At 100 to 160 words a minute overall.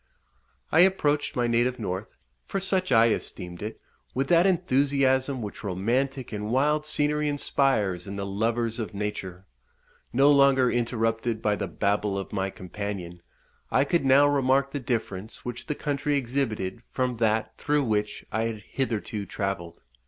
Yes: average, 150 wpm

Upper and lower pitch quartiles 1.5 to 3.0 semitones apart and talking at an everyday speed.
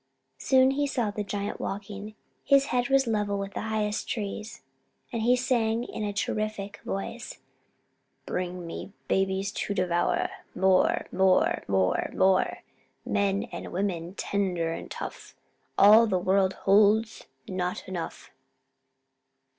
No: narrow, 2.6 semitones; slow, 130 wpm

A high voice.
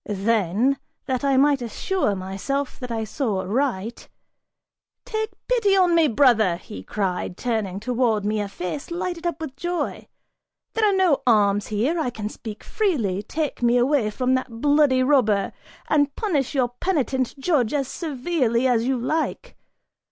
Yes: very high, 255 Hz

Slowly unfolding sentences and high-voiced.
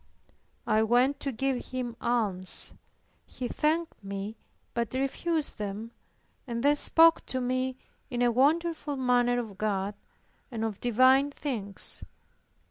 Yes: slow, 125 wpm; high, 245 Hz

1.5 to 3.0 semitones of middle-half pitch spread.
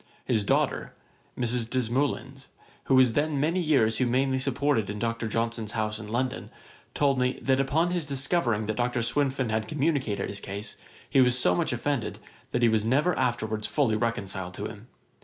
No: average, 3.8 semitones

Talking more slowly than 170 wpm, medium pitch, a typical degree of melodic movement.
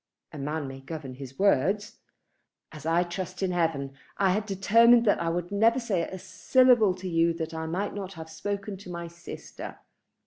No: average, 185 wpm; medium, 180 Hz; average, 3.8 semitones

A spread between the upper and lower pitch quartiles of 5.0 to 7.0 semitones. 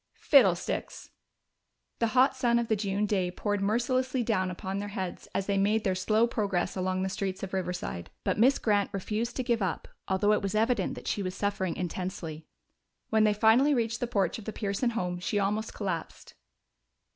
No: average, 3.2 semitones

